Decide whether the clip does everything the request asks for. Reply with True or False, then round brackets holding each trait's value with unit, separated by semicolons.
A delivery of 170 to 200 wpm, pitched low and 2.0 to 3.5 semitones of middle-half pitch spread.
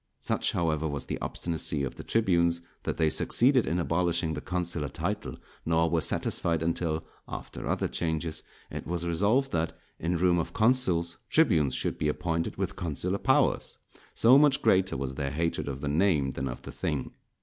True (175 wpm; 85 Hz; 2.9 semitones)